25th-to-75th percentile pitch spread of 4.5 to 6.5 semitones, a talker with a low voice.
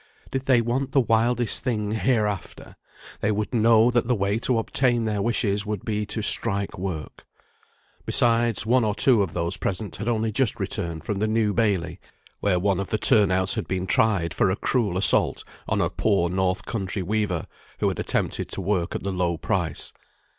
No: average, 3.3 semitones; low, 105 Hz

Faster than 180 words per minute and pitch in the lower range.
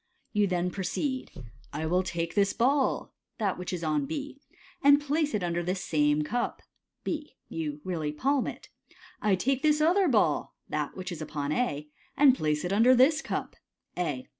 No: average, 195 wpm; medium, 185 Hz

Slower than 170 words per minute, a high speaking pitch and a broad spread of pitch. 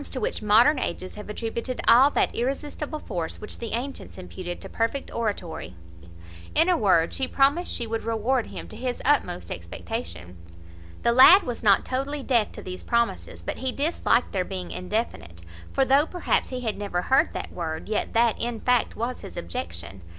No: average, 180 wpm; high, 230 Hz; wide, 6.2 semitones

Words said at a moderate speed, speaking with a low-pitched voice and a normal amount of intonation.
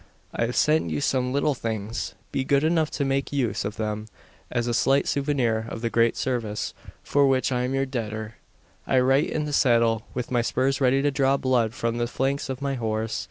No: fast, 210 wpm; low, 125 Hz; average, 3.0 semitones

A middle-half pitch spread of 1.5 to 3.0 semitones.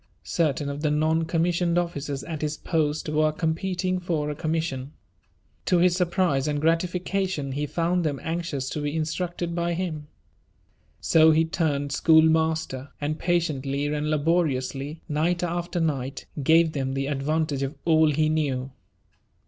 Yes: average, 2.7 semitones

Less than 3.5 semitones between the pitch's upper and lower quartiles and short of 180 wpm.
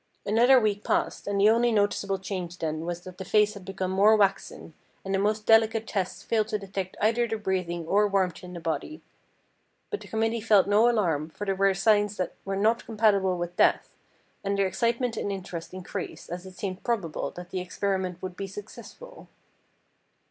No: average, 2.8 semitones; average, 190 wpm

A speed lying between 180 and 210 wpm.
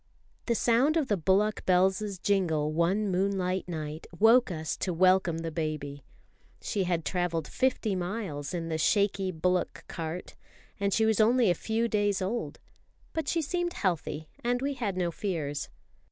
No: average, 160 wpm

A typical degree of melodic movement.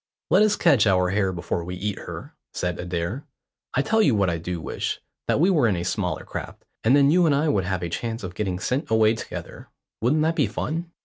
No: wide, 8.3 semitones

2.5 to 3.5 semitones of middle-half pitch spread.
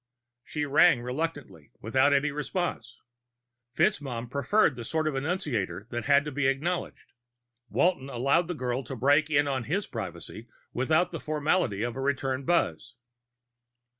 No: average, 4.0 semitones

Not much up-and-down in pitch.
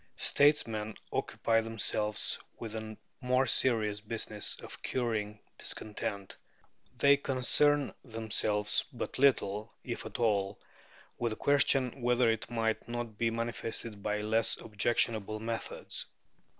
Yes: narrow, 2.3 semitones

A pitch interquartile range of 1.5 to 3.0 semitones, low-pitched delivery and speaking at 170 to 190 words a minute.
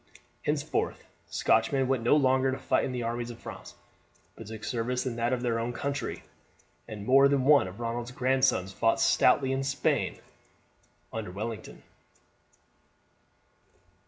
No: narrow, 2.5 semitones; low, 120 Hz; average, 145 wpm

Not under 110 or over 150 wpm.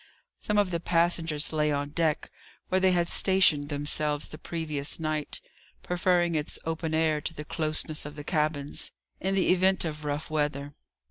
No: average, 170 wpm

